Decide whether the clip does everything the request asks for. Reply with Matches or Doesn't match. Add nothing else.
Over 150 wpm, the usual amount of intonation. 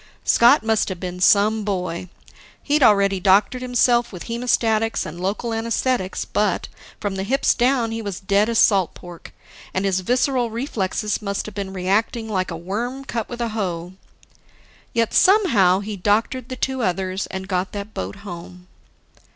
Matches